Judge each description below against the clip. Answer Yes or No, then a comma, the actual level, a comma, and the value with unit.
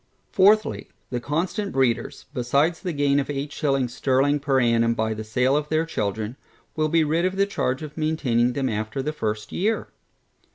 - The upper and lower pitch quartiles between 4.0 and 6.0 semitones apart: Yes, average, 4.6 semitones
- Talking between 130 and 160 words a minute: No, average, 180 wpm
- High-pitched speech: No, medium, 140 Hz